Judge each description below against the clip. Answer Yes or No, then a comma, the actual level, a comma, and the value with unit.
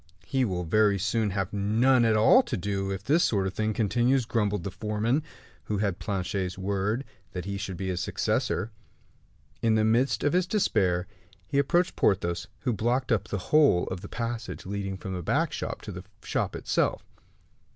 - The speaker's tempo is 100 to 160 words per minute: No, average, 185 wpm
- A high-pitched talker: No, low, 105 Hz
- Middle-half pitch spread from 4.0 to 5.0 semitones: No, average, 3.6 semitones